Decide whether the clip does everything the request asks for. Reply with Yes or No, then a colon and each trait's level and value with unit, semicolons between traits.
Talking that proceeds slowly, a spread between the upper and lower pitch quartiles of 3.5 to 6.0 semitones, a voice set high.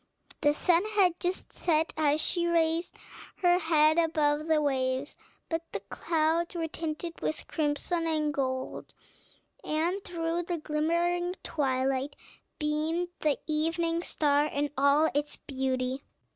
No: slow, 130 wpm; narrow, 2.5 semitones; very high, 315 Hz